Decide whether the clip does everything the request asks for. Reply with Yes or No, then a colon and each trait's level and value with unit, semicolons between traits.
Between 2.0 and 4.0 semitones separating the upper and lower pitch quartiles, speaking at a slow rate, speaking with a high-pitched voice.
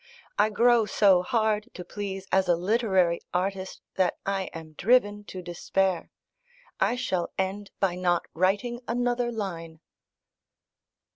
Yes: average, 3.2 semitones; slow, 130 wpm; high, 195 Hz